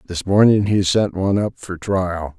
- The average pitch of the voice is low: Yes, very low, 95 Hz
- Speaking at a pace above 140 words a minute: Yes, average, 200 wpm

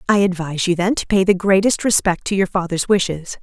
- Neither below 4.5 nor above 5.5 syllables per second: No, 5.9 syllables/s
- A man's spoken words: No, female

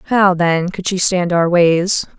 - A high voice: No, medium, 180 Hz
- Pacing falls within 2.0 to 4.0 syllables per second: Yes, 3.7 syllables/s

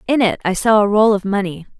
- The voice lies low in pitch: No, high, 205 Hz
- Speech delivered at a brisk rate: Yes, fast, 265 wpm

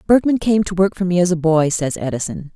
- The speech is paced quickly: Yes, fast, 260 wpm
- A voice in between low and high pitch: Yes, medium, 175 Hz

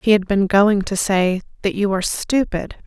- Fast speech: Yes, fast, 210 wpm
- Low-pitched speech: No, high, 200 Hz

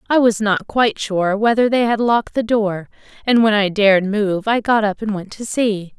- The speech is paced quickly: Yes, fast, 230 wpm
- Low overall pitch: No, high, 215 Hz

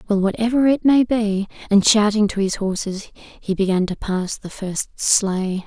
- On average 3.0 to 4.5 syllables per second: Yes, 4.3 syllables/s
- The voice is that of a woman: Yes, female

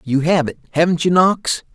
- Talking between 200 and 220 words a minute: Yes, fast, 205 wpm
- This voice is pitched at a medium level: Yes, medium, 165 Hz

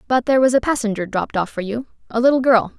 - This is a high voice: Yes, high, 235 Hz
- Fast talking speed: Yes, fast, 235 wpm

